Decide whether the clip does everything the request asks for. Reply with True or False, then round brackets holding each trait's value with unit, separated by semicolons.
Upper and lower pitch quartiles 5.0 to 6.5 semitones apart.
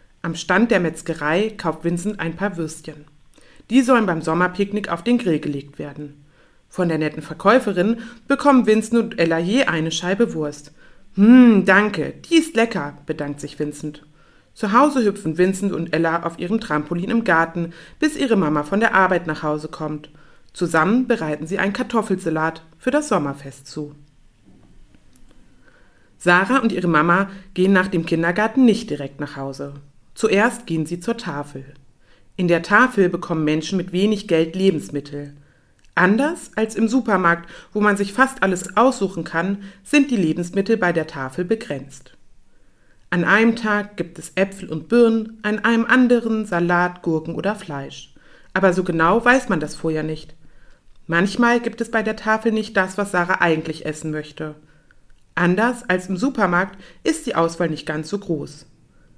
True (5.6 semitones)